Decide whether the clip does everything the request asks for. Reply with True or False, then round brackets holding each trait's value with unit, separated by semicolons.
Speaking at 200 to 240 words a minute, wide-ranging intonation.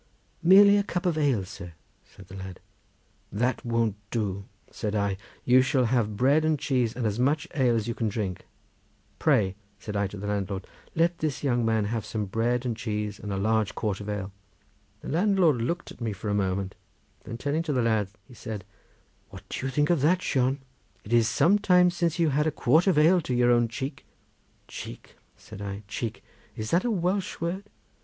True (205 wpm; 6.6 semitones)